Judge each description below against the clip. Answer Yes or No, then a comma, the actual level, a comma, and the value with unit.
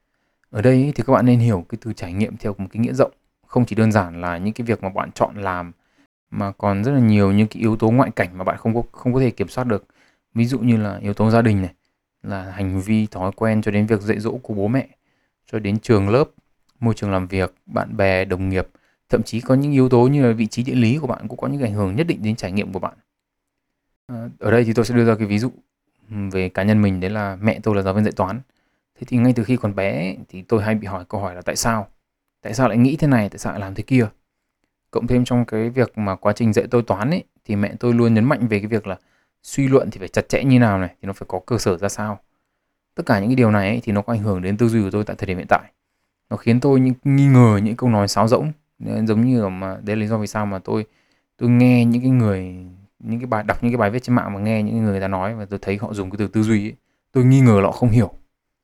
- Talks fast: Yes, fast, 290 wpm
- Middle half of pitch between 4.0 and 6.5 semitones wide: No, average, 3.3 semitones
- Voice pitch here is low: Yes, low, 110 Hz